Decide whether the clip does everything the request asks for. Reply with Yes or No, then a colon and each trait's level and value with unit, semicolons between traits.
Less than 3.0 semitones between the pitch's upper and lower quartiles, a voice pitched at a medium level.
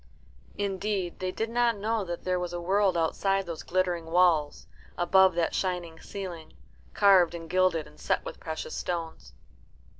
Yes: narrow, 2.5 semitones; medium, 180 Hz